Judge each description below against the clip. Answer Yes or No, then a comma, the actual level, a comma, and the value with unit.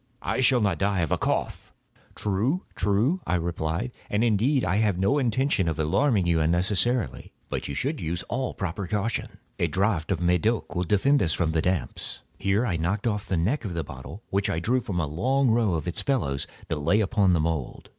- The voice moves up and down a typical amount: No, wide, 5.7 semitones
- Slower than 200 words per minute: No, fast, 205 wpm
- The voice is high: No, low, 100 Hz